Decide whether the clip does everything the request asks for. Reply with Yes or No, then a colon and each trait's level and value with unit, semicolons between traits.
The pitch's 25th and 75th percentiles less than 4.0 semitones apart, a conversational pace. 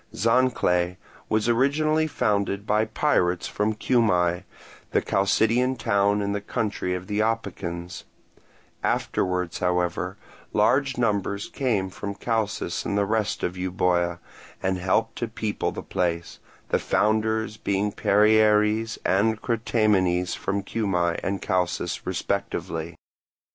No: average, 3.4 semitones; slow, 115 wpm